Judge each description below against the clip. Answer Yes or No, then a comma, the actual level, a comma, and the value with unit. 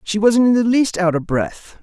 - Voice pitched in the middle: No, high, 205 Hz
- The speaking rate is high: Yes, fast, 260 wpm